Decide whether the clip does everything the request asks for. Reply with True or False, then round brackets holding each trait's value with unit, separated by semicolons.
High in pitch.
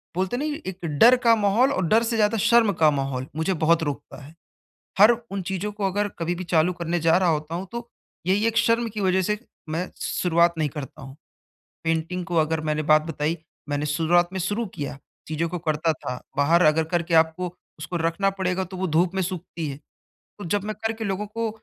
False (175 Hz)